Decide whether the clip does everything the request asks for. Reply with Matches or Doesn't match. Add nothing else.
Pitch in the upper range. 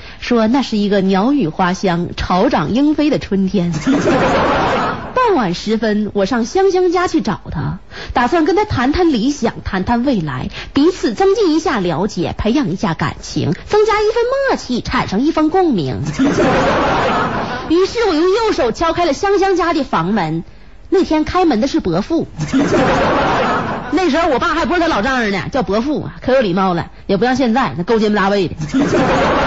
Matches